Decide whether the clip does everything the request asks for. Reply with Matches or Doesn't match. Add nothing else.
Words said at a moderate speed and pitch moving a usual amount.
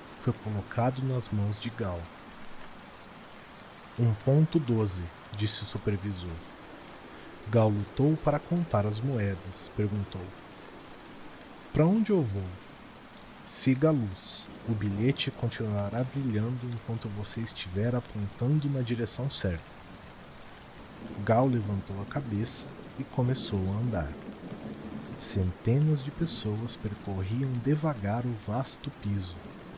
Doesn't match